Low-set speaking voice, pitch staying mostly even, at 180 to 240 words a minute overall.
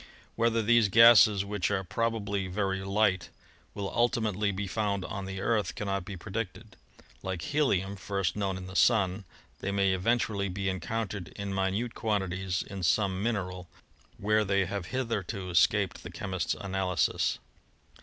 No: low, 100 Hz; narrow, 2.2 semitones; average, 150 wpm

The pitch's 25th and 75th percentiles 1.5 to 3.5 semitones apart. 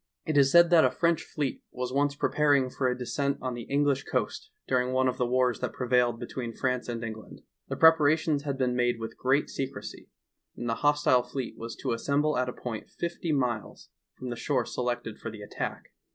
Yes: average, 2.9 semitones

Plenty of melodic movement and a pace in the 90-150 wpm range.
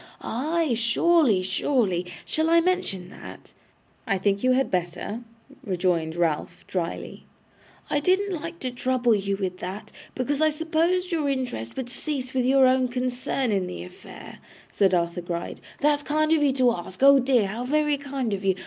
No: wide, 7.3 semitones; average, 170 wpm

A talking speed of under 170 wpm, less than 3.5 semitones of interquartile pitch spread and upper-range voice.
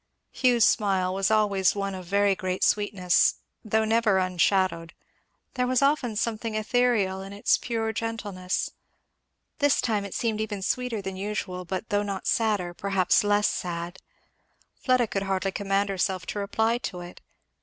Yes: average, 155 wpm; average, 2.8 semitones; high, 200 Hz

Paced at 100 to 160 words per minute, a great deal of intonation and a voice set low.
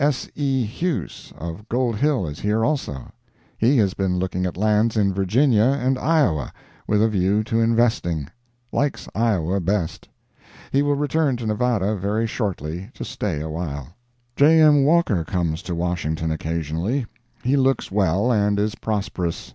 Yes: average, 155 wpm; wide, 6.0 semitones; low, 105 Hz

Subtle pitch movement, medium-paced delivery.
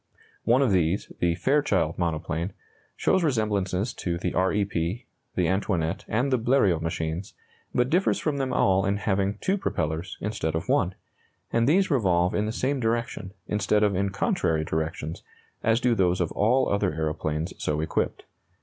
No: wide, 5.4 semitones; average, 170 wpm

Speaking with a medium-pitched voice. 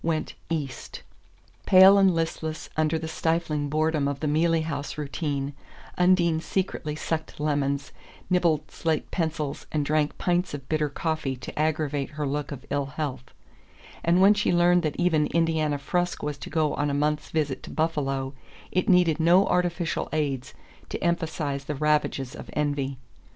Yes: medium, 155 Hz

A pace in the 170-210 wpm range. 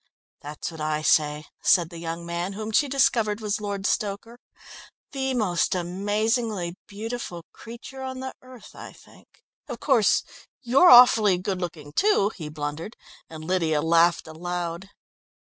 No: average, 145 wpm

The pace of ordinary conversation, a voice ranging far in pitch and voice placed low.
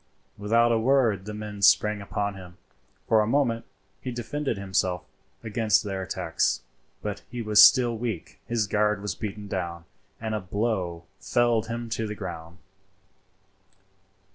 No: average, 145 wpm; average, 2.9 semitones; low, 105 Hz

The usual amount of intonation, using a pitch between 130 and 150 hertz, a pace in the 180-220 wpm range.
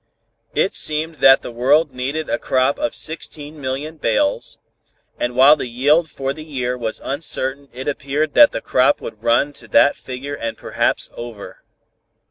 No: average, 3.1 semitones; medium, 140 Hz; average, 160 wpm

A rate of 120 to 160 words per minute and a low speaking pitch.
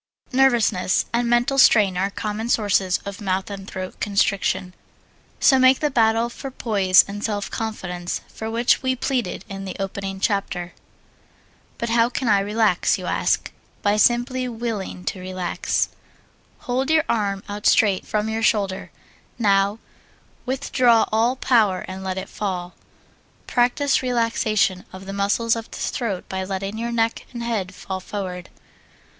No: average, 150 wpm; high, 210 Hz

